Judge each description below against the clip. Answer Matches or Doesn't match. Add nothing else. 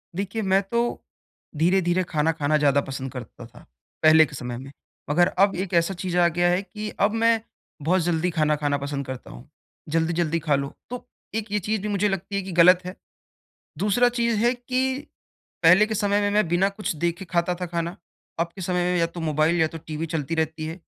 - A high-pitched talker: Doesn't match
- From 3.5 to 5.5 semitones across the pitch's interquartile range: Matches